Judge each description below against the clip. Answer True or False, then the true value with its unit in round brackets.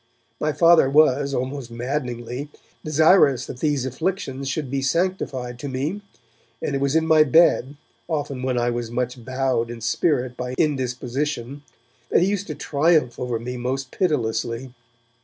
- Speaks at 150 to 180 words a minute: True (155 wpm)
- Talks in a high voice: False (135 Hz)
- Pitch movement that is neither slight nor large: True (3.5 semitones)